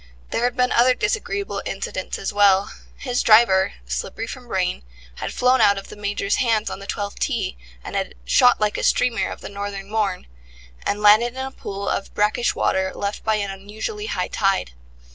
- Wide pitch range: No, average, 3.7 semitones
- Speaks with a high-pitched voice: Yes, high, 210 Hz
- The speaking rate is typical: Yes, average, 190 wpm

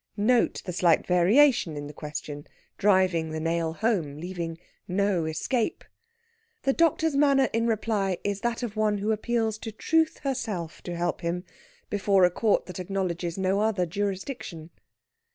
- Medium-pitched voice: No, high, 195 Hz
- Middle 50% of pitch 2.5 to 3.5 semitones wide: No, average, 4.7 semitones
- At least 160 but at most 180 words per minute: No, average, 150 wpm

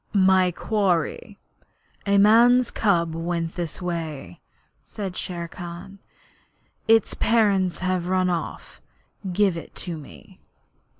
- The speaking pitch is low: No, medium, 185 Hz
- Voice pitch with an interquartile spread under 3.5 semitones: Yes, average, 2.9 semitones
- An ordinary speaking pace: No, slow, 110 wpm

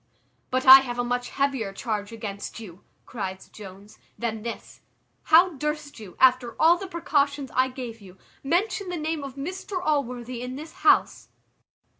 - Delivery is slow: No, average, 160 wpm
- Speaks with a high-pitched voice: Yes, very high, 255 Hz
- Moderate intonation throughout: Yes, average, 5.0 semitones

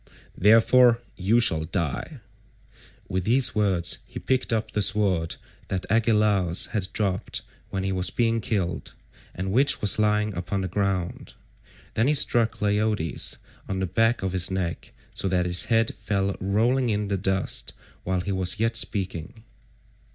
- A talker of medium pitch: No, low, 100 Hz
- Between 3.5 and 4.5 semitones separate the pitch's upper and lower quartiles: No, average, 3.1 semitones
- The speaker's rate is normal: Yes, average, 155 wpm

